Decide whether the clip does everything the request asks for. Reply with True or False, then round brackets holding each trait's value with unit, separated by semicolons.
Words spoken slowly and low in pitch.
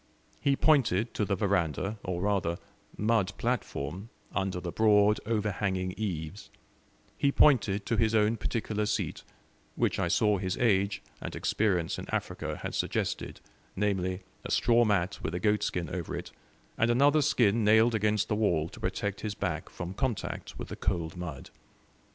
False (155 wpm; 100 Hz)